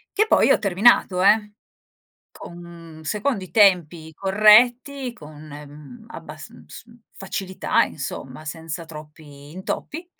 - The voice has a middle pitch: Yes, medium, 180 Hz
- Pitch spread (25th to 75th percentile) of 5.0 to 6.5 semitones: Yes, wide, 5.5 semitones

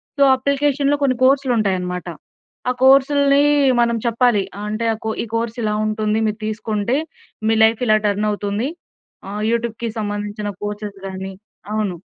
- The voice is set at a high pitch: Yes, high, 220 Hz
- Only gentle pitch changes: No, average, 3.4 semitones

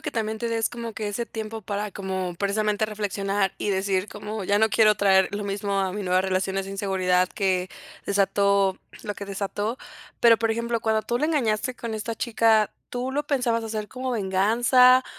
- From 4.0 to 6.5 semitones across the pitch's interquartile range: No, narrow, 2.6 semitones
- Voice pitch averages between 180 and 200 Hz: No, high, 210 Hz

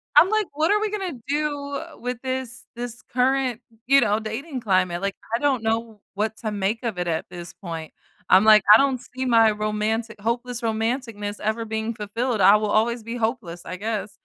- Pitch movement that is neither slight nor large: Yes, average, 3.3 semitones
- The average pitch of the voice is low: No, high, 225 Hz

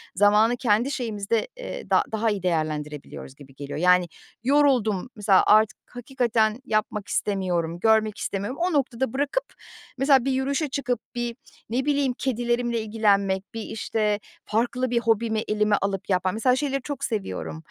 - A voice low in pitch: No, high, 220 Hz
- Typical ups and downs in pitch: Yes, average, 4.2 semitones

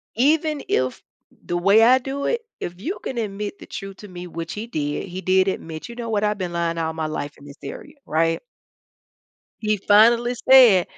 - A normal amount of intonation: No, wide, 5.8 semitones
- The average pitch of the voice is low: No, high, 195 Hz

